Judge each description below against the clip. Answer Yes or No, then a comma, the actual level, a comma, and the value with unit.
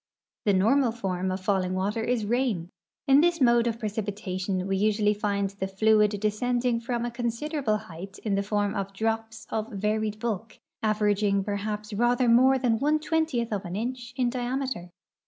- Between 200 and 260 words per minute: No, average, 175 wpm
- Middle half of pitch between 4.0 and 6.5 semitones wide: No, average, 3.2 semitones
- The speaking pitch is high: Yes, high, 215 Hz